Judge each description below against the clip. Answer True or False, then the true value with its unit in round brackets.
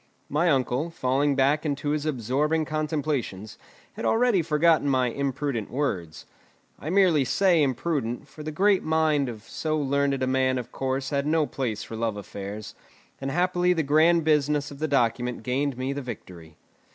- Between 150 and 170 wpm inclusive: True (165 wpm)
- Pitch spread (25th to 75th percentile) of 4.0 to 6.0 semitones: False (3.5 semitones)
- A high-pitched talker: False (140 Hz)